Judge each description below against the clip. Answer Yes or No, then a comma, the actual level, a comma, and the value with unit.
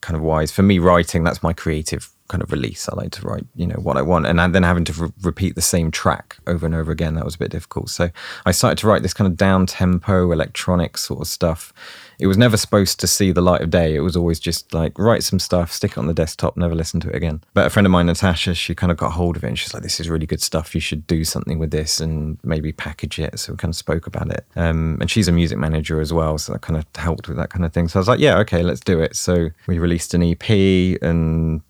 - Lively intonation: No, narrow, 2.4 semitones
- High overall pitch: No, very low, 85 Hz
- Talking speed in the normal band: No, fast, 290 wpm